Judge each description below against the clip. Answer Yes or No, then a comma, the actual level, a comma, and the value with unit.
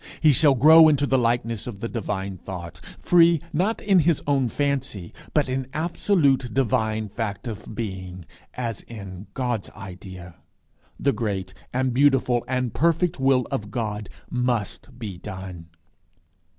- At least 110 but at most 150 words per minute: Yes, average, 140 wpm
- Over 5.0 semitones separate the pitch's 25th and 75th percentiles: Yes, wide, 5.4 semitones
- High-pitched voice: No, low, 120 Hz